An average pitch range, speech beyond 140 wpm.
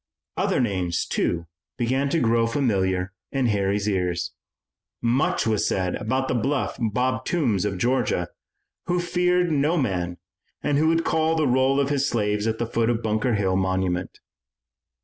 No: wide, 6.1 semitones; average, 160 wpm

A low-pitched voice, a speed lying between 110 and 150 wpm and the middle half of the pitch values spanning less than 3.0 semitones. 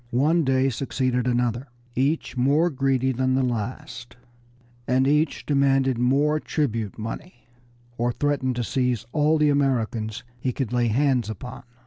Yes: low, 130 Hz; average, 140 wpm; narrow, 2.6 semitones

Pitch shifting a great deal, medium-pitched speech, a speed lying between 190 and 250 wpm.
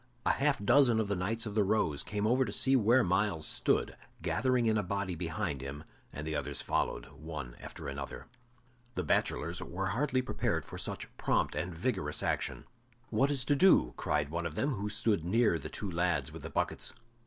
No: wide, 6.6 semitones; low, 100 Hz; average, 195 wpm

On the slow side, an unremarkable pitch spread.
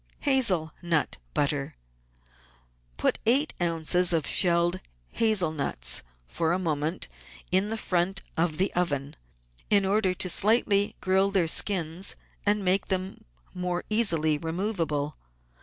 Yes: slow, 125 wpm; average, 3.6 semitones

